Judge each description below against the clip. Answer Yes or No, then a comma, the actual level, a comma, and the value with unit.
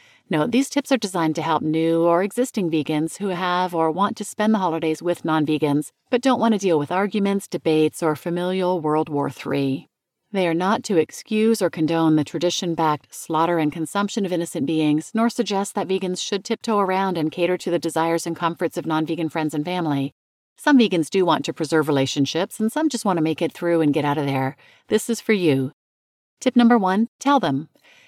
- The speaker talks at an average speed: No, fast, 215 wpm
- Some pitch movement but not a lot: Yes, average, 4.5 semitones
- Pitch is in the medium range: Yes, medium, 170 Hz